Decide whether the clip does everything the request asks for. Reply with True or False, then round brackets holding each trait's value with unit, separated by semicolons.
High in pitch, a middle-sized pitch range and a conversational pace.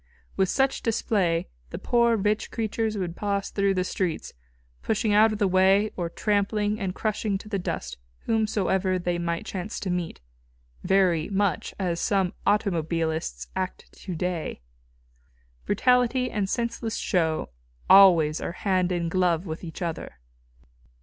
True (195 Hz; 3.3 semitones; 145 wpm)